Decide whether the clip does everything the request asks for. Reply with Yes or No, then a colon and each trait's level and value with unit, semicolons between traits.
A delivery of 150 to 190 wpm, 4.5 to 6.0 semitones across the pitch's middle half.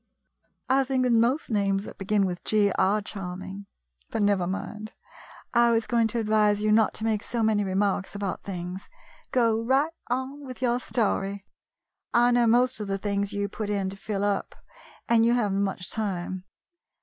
No: average, 185 wpm; average, 3.0 semitones